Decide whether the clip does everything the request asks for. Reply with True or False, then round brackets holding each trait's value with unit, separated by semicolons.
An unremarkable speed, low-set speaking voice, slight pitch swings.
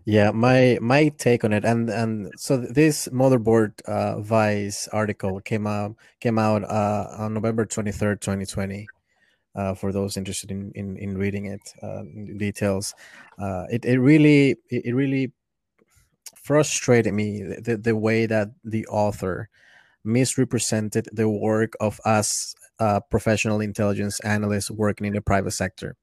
True (145 wpm; 105 Hz; 2.3 semitones)